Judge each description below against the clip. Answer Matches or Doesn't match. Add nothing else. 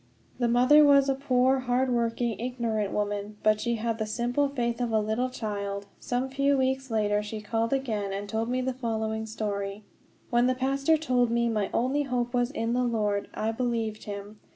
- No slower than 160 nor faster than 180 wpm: Doesn't match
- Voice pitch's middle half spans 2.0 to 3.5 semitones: Matches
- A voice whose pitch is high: Matches